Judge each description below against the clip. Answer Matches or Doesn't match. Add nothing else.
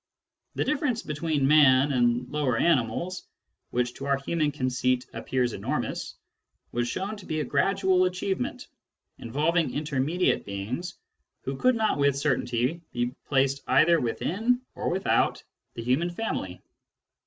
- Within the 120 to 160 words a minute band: Matches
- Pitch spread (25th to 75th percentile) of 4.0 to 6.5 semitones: Matches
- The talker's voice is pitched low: Doesn't match